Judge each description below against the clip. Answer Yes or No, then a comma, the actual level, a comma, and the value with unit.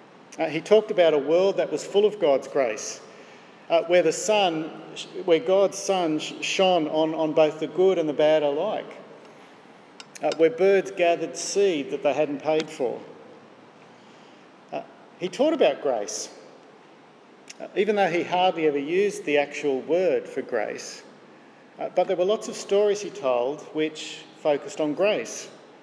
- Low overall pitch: No, medium, 170 Hz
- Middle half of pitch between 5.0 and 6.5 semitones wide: No, average, 4.1 semitones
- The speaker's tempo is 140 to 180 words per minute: Yes, average, 160 wpm